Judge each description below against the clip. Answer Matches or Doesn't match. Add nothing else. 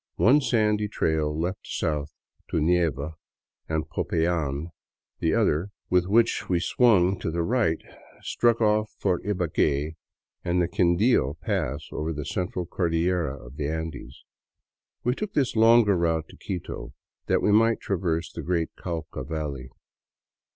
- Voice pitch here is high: Doesn't match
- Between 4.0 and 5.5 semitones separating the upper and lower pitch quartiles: Matches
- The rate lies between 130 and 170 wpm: Matches